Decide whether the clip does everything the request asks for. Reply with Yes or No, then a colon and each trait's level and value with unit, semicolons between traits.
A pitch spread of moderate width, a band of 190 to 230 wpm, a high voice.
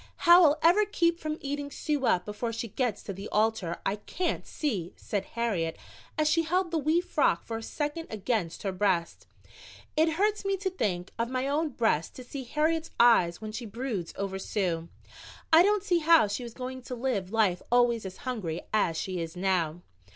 No: wide, 8.1 semitones; average, 200 wpm; high, 235 Hz